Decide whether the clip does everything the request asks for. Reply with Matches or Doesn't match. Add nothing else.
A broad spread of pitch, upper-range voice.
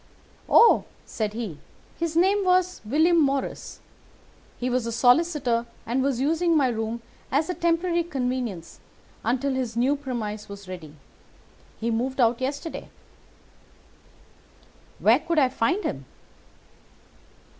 Matches